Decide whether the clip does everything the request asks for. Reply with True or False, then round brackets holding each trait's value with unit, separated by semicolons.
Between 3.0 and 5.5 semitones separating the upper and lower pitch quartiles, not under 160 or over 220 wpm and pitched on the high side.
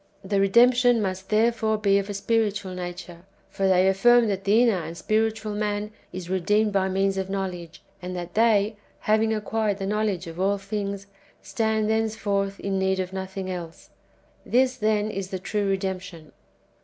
False (2.4 semitones; 170 wpm; 200 Hz)